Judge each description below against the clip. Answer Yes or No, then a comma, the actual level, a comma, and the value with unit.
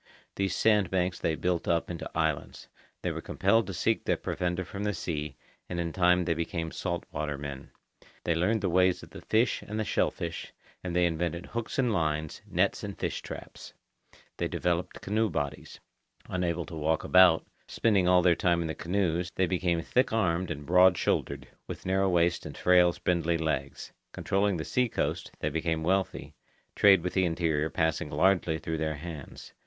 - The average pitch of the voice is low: Yes, very low, 90 Hz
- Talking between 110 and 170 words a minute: No, average, 185 wpm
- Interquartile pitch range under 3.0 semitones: Yes, narrow, 2.5 semitones